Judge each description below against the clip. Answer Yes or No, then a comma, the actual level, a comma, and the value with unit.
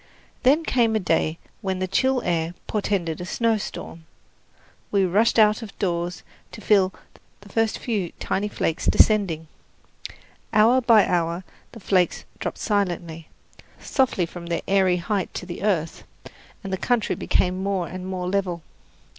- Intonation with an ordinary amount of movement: Yes, average, 3.5 semitones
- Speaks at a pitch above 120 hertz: Yes, high, 190 Hz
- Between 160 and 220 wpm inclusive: No, average, 145 wpm